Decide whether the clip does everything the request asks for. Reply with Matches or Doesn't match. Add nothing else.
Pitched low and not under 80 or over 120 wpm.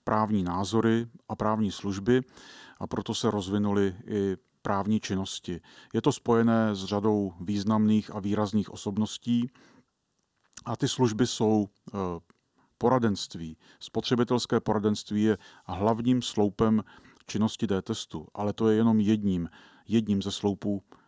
Matches